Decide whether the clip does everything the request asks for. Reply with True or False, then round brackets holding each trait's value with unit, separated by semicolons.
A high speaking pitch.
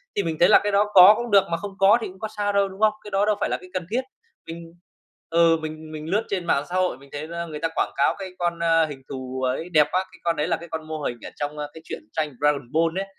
False (165 Hz)